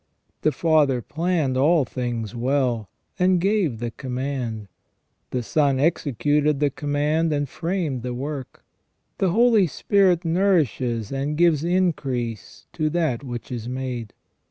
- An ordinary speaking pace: No, slow, 130 wpm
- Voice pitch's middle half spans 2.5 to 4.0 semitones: No, average, 4.9 semitones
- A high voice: No, medium, 145 Hz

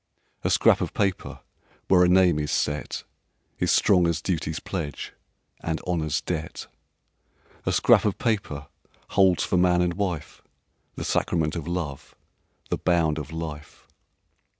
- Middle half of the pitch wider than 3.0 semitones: No, average, 2.7 semitones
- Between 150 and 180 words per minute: No, average, 140 wpm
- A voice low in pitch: Yes, very low, 85 Hz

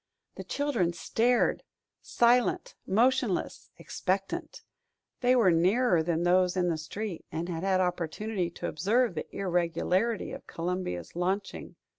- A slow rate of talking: Yes, slow, 125 wpm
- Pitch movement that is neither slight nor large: Yes, average, 4.6 semitones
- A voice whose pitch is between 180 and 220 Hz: Yes, medium, 185 Hz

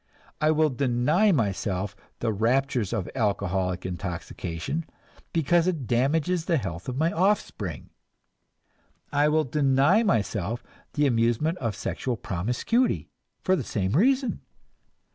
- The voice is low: Yes, low, 130 Hz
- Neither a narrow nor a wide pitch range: No, wide, 7.8 semitones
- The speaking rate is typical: No, slow, 120 wpm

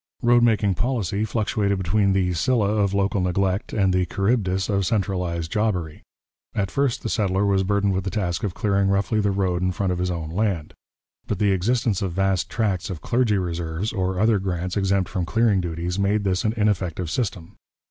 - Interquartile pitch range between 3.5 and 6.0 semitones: No, narrow, 2.5 semitones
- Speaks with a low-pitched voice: Yes, very low, 95 Hz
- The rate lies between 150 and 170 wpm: No, average, 190 wpm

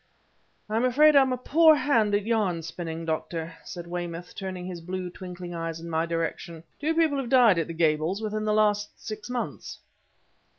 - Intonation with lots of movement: Yes, wide, 5.7 semitones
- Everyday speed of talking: Yes, average, 180 wpm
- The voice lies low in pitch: No, medium, 185 Hz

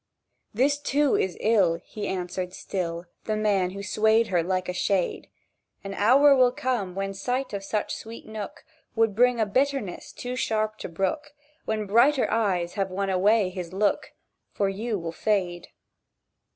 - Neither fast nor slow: Yes, average, 165 wpm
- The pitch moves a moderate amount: Yes, average, 3.7 semitones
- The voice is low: No, high, 205 Hz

